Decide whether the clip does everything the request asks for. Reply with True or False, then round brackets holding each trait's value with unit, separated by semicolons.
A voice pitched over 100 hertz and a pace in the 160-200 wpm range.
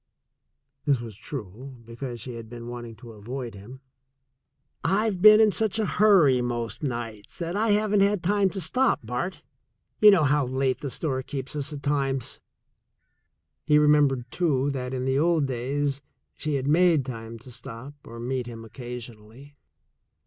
True (135 Hz; 165 wpm)